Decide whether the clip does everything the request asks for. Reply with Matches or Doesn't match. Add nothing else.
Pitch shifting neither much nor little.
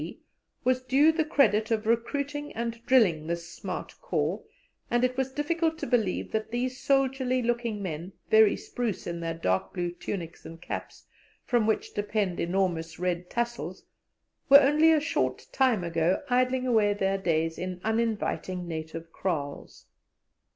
Doesn't match